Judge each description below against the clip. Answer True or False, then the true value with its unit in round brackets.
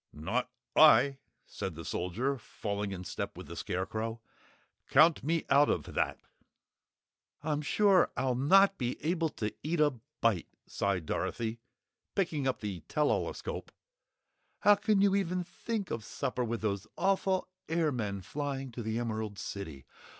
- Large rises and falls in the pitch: True (7.3 semitones)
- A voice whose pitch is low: True (130 Hz)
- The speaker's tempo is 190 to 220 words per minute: False (150 wpm)